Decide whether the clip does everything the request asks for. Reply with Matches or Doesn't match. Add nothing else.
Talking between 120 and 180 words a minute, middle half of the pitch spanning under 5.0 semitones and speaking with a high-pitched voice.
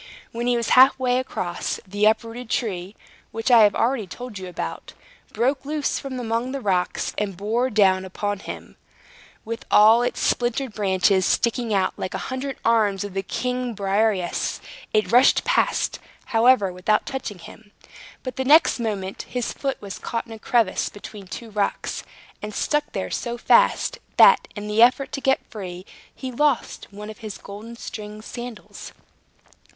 Matches